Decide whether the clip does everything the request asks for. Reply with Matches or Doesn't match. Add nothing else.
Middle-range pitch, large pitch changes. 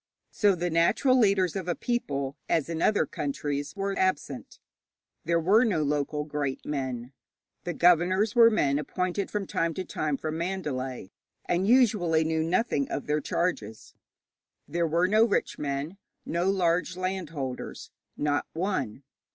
Doesn't match